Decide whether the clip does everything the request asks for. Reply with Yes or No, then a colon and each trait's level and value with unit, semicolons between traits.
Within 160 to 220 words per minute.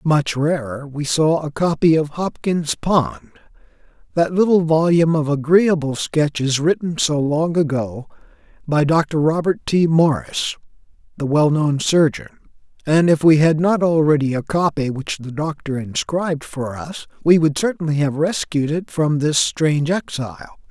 No: average, 150 wpm